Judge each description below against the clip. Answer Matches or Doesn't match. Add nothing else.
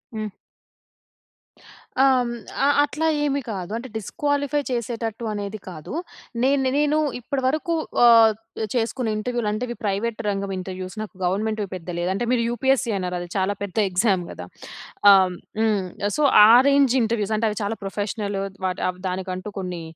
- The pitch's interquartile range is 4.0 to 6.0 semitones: Matches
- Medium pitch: Doesn't match